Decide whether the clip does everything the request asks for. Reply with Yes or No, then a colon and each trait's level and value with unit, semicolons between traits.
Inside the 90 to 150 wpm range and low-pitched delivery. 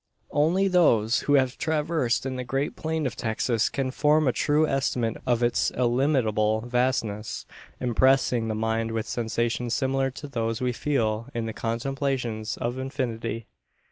Yes: average, 145 wpm; low, 125 Hz